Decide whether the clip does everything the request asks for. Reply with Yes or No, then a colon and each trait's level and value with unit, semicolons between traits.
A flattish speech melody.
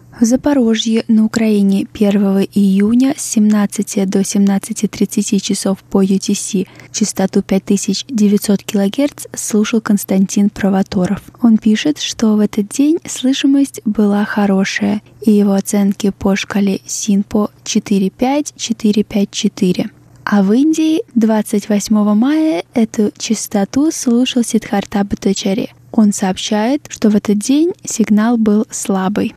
Yes: narrow, 2.3 semitones